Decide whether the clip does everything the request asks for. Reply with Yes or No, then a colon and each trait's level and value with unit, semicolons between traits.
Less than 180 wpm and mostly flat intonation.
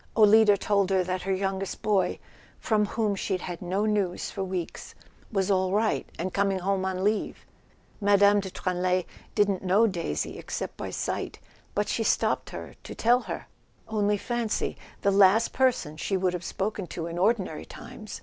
Yes: average, 170 wpm; narrow, 2.2 semitones